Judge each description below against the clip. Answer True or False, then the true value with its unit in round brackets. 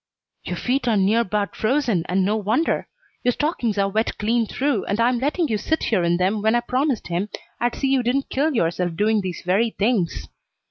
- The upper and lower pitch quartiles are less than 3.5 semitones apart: False (4.3 semitones)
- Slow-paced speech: False (205 wpm)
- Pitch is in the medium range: False (220 Hz)